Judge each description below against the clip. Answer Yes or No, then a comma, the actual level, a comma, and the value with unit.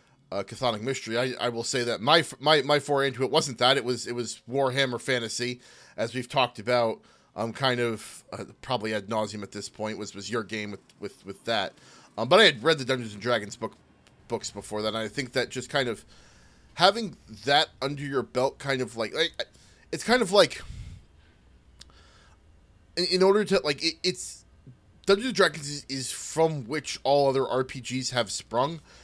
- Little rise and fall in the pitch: No, average, 4.1 semitones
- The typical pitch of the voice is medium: No, low, 125 Hz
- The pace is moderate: Yes, average, 195 wpm